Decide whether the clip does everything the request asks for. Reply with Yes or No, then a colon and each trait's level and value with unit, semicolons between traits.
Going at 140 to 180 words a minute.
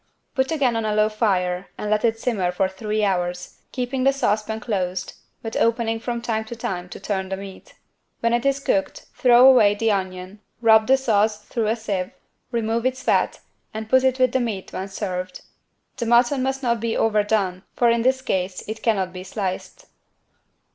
No: average, 190 wpm